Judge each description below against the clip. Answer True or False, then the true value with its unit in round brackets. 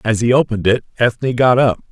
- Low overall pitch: True (120 Hz)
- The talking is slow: False (220 wpm)